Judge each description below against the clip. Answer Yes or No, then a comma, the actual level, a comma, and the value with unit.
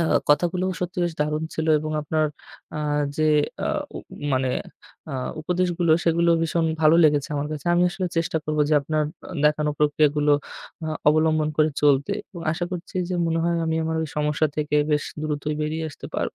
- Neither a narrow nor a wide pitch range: No, narrow, 1.8 semitones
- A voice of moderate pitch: Yes, medium, 155 Hz